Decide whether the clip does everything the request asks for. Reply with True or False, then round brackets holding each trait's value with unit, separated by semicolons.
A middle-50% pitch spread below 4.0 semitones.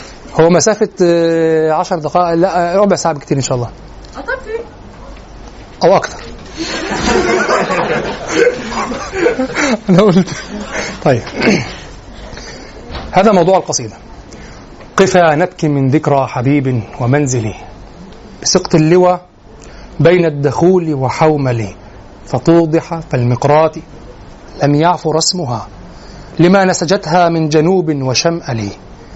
False (5.6 semitones)